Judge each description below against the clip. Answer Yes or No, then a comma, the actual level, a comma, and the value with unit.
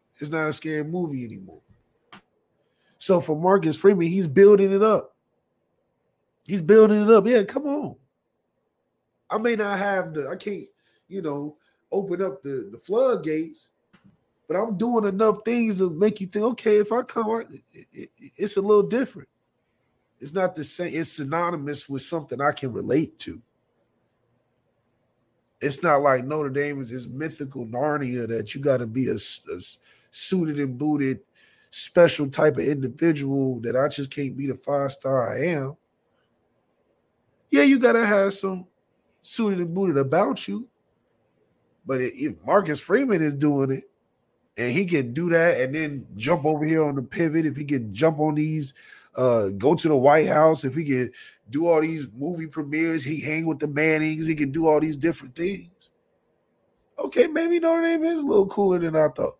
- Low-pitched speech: No, medium, 155 Hz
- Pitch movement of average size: No, wide, 5.8 semitones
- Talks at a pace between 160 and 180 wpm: Yes, average, 175 wpm